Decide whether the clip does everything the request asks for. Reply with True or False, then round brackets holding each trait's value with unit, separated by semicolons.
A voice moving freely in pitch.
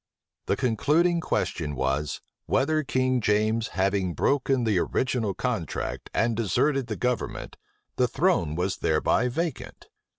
True (5.8 semitones)